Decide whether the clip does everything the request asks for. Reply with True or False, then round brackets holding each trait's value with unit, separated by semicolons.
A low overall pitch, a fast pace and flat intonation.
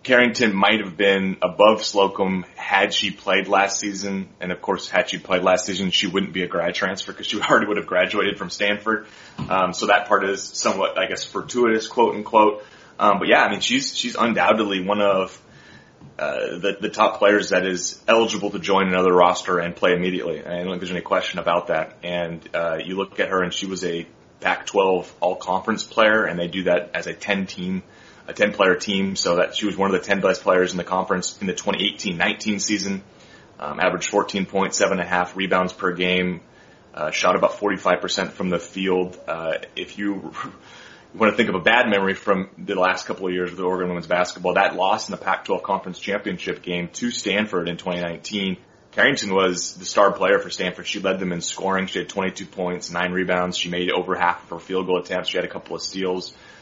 True (95 Hz; 210 wpm; 1.9 semitones)